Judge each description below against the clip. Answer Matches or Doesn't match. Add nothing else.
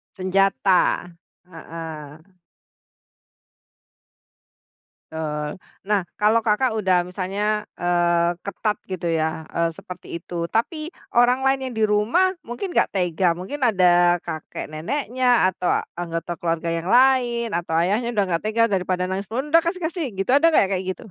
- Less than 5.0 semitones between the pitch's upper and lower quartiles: Doesn't match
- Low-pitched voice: Doesn't match